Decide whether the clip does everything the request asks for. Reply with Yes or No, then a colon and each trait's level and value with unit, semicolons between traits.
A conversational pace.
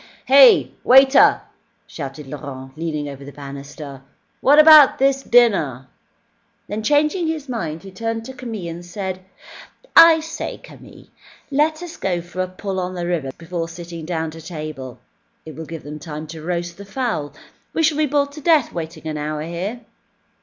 Yes: average, 170 wpm